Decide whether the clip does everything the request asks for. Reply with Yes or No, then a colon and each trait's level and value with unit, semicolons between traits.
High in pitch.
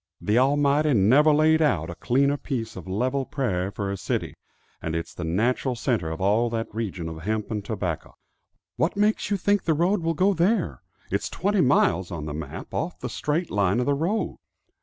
No: low, 120 Hz